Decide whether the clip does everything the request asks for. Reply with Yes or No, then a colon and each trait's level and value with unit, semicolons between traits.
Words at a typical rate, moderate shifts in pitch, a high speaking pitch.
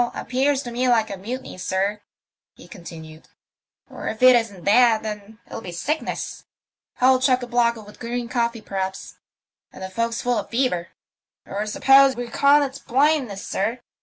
Yes: average, 170 wpm; average, 4.0 semitones; high, 235 Hz